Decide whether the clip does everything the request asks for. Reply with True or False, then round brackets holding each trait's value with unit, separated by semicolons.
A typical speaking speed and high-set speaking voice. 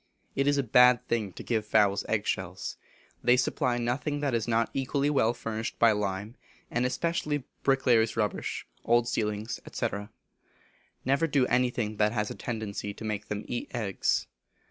False (165 wpm; 115 Hz)